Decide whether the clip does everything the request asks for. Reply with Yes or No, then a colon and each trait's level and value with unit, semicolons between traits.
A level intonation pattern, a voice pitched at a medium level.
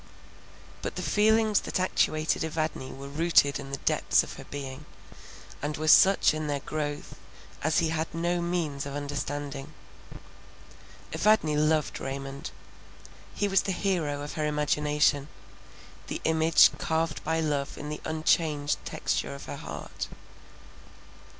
Yes: narrow, 2.2 semitones; medium, 150 Hz